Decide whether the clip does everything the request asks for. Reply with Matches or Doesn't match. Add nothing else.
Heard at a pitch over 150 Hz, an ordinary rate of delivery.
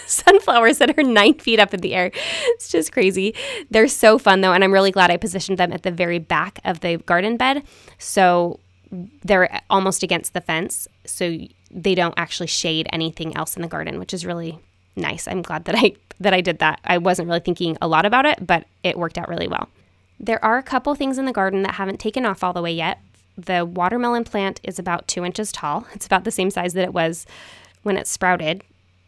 Doesn't match